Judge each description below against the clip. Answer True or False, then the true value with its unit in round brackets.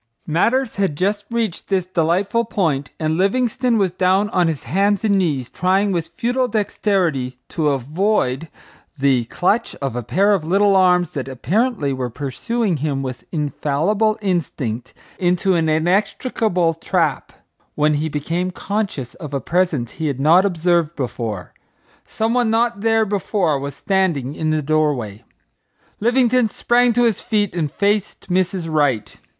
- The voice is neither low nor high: True (175 Hz)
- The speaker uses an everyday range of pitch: False (5.8 semitones)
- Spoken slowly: False (150 wpm)